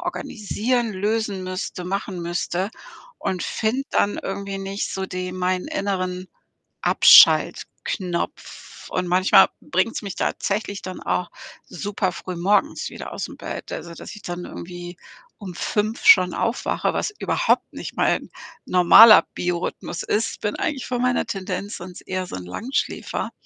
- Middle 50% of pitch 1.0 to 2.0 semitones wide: No, narrow, 2.6 semitones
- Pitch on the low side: No, high, 190 Hz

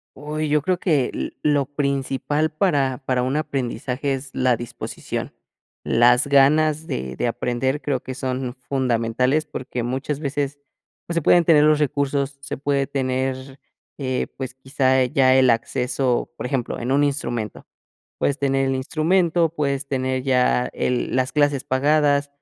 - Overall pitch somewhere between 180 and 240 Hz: No, low, 135 Hz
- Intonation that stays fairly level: Yes, narrow, 2.2 semitones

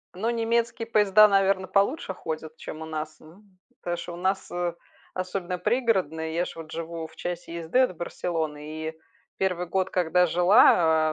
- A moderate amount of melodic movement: Yes, average, 3.3 semitones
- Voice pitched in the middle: Yes, medium, 175 Hz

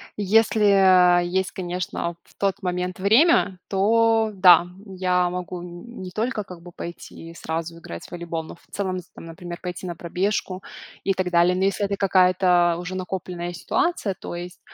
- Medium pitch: Yes, medium, 180 Hz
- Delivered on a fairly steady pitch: Yes, narrow, 1.9 semitones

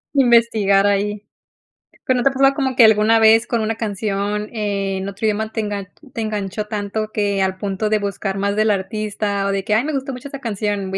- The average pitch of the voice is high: Yes, high, 210 Hz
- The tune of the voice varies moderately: No, narrow, 2.1 semitones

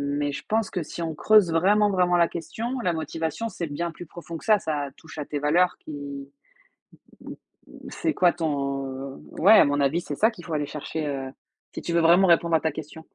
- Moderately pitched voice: Yes, medium, 165 Hz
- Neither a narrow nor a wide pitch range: Yes, average, 3.6 semitones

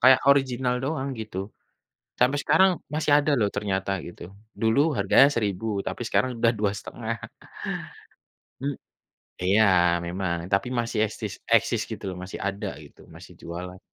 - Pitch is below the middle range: Yes, low, 115 Hz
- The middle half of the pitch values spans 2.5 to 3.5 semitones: No, average, 5.2 semitones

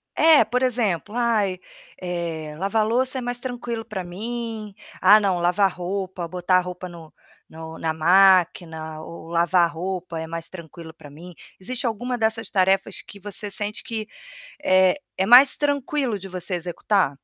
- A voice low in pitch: No, high, 190 Hz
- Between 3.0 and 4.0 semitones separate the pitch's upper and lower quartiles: No, average, 4.5 semitones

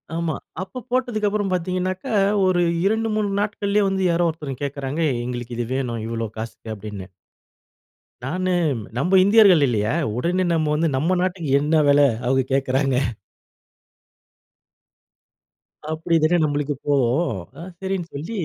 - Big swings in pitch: Yes, wide, 5.8 semitones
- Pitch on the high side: No, medium, 160 Hz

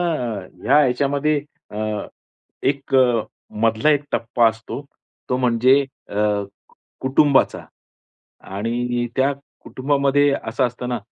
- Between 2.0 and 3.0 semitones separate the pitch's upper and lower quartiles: No, average, 3.4 semitones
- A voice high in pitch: No, low, 125 Hz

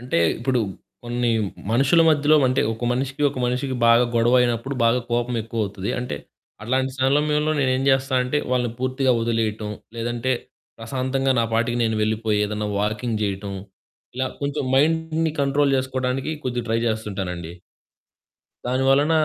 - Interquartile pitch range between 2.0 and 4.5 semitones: Yes, average, 2.8 semitones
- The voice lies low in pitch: Yes, low, 125 Hz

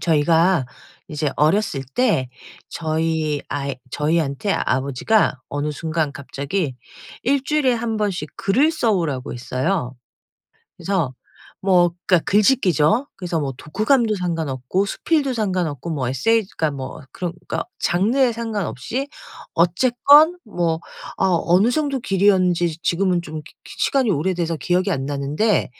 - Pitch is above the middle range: No, medium, 175 Hz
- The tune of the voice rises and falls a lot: Yes, wide, 6.2 semitones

